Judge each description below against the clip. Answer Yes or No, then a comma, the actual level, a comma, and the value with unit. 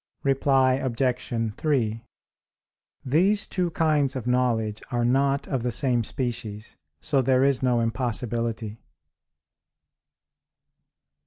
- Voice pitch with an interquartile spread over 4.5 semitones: No, average, 2.8 semitones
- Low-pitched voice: Yes, low, 125 Hz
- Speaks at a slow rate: Yes, slow, 100 wpm